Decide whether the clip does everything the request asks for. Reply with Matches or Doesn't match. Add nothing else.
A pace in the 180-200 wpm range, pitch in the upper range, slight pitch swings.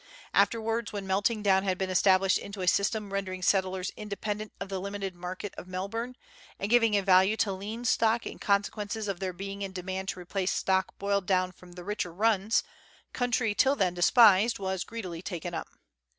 Matches